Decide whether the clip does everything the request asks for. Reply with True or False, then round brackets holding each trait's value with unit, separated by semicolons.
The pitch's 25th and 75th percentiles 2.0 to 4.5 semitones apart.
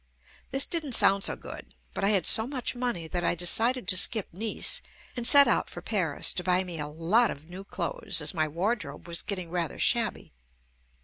False (5.4 semitones)